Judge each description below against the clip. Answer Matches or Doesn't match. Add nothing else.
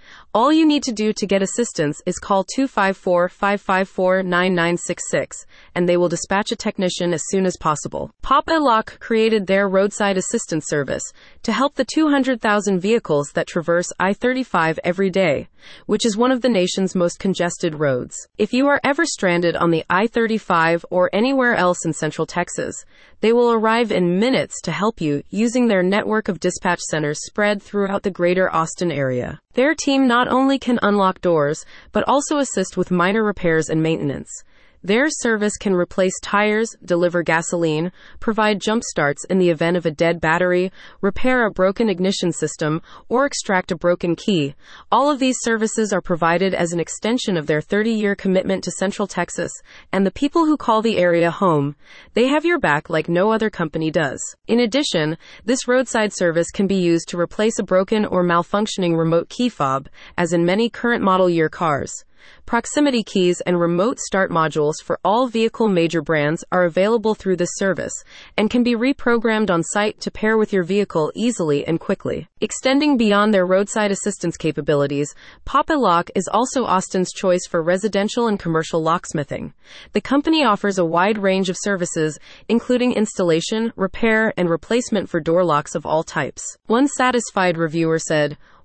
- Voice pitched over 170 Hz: Matches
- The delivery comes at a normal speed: Matches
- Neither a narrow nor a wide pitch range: Matches